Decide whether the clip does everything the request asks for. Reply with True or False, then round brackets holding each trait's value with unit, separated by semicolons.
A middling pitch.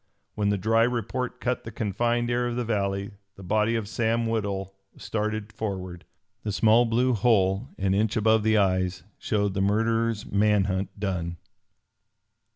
False (105 Hz)